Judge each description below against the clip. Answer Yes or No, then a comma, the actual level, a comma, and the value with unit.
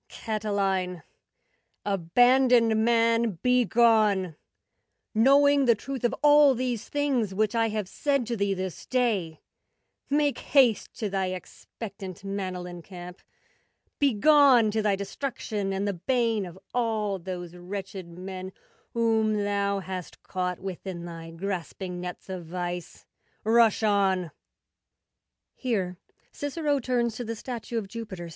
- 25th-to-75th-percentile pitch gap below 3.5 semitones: No, average, 4.1 semitones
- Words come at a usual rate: No, slow, 105 wpm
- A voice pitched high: Yes, high, 205 Hz